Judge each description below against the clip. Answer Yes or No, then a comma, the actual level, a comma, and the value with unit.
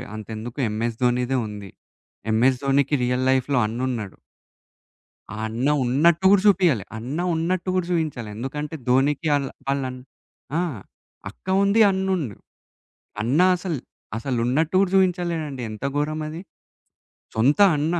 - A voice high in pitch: No, medium, 140 Hz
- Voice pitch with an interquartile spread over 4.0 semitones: Yes, average, 5.1 semitones